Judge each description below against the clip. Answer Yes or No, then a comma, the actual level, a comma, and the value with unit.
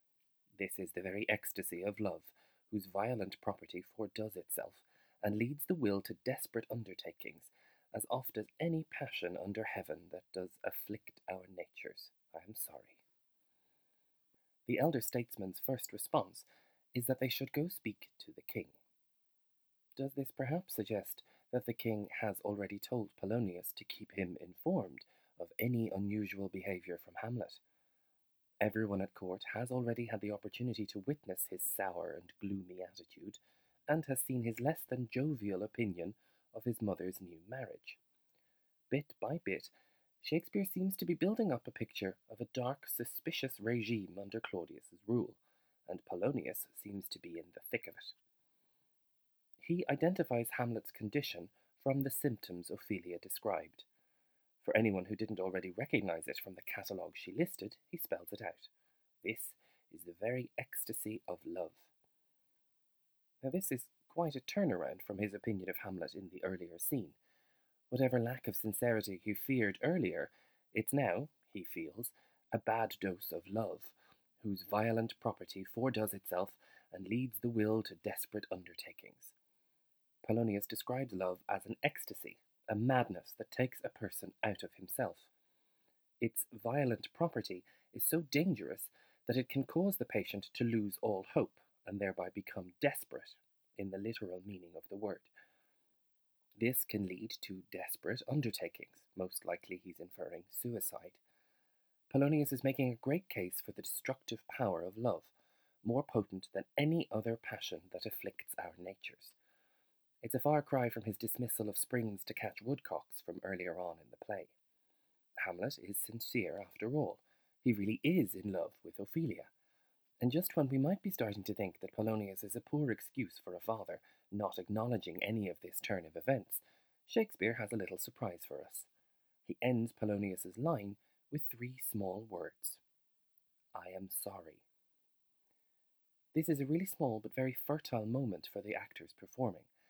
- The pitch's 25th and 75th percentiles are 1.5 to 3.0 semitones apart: No, average, 4.6 semitones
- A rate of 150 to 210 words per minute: Yes, average, 155 wpm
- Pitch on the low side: Yes, low, 115 Hz